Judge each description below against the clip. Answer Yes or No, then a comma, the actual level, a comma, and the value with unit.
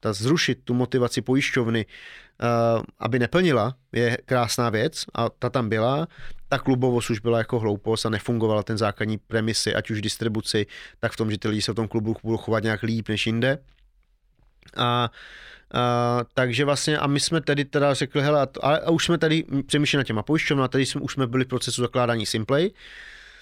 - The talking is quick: Yes, fast, 185 wpm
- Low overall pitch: Yes, low, 120 Hz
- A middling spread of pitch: Yes, average, 3.6 semitones